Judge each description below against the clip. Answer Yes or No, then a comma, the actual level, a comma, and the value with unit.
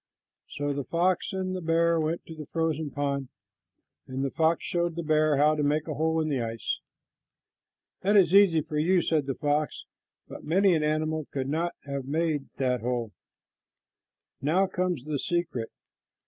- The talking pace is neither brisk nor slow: Yes, average, 175 wpm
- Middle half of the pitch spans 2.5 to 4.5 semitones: Yes, average, 2.9 semitones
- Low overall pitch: No, medium, 155 Hz